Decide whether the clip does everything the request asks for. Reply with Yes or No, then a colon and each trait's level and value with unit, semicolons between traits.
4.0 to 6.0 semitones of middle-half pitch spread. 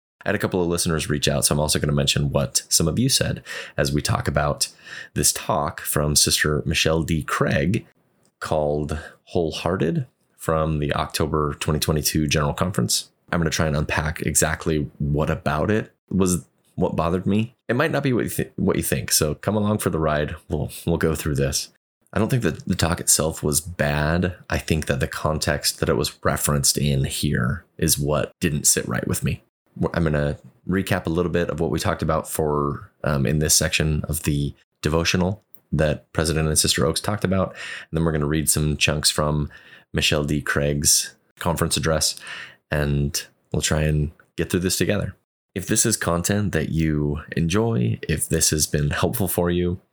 No: average, 2.9 semitones